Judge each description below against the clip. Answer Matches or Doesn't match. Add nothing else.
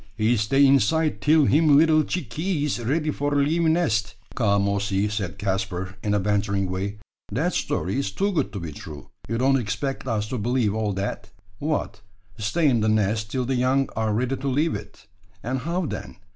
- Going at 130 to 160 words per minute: Doesn't match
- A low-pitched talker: Matches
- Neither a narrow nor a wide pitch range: Doesn't match